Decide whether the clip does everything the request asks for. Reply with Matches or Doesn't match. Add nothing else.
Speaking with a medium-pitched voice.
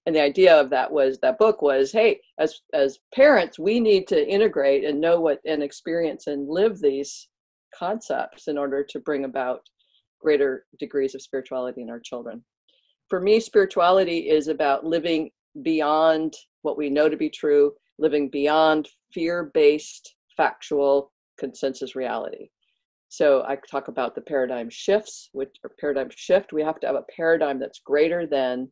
Matches